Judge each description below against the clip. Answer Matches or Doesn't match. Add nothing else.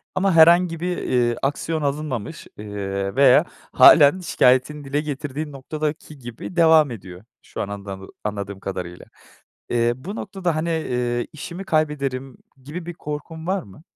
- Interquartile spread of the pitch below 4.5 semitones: Doesn't match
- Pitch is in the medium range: Matches